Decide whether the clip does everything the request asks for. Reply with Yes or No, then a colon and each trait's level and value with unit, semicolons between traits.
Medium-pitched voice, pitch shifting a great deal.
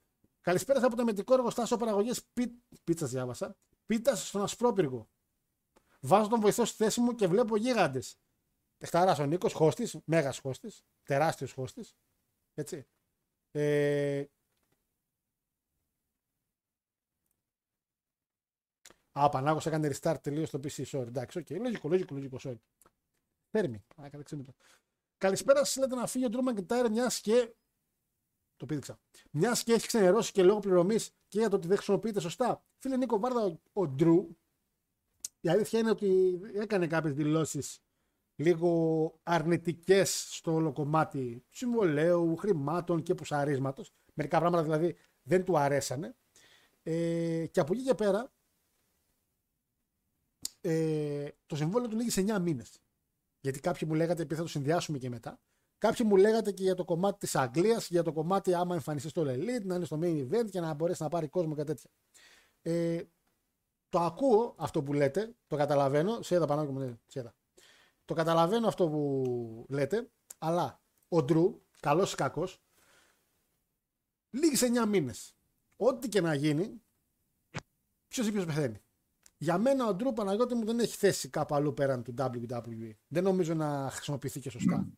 Yes: medium, 170 Hz; wide, 5.8 semitones